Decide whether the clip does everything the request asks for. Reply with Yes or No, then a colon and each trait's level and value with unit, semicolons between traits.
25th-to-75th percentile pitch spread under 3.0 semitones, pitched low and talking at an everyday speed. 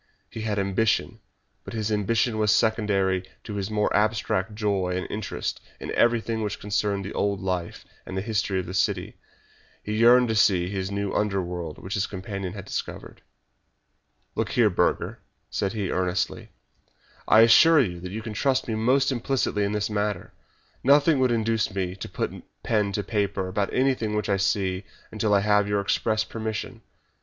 Yes: narrow, 2.4 semitones; low, 105 Hz; average, 170 wpm